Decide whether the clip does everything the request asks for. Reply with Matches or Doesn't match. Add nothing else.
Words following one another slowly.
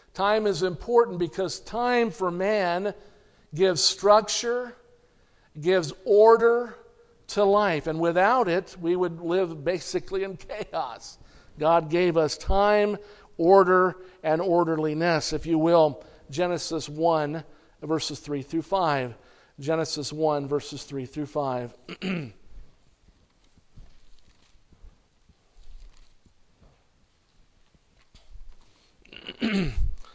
Matches